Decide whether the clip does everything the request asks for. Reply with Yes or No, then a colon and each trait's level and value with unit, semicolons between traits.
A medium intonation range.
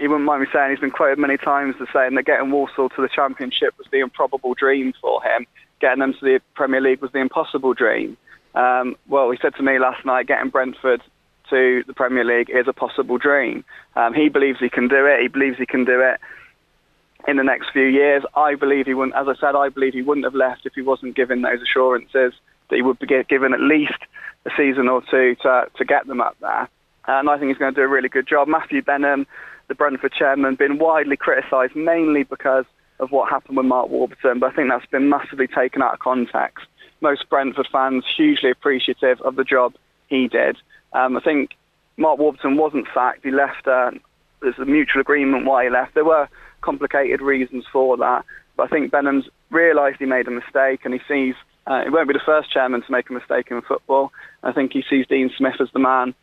No: narrow, 1.7 semitones